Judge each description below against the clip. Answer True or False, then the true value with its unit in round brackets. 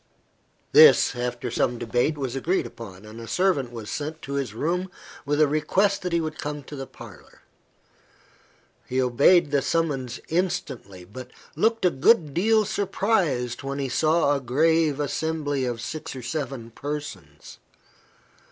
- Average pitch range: True (4.9 semitones)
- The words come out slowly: False (150 wpm)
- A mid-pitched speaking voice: True (145 Hz)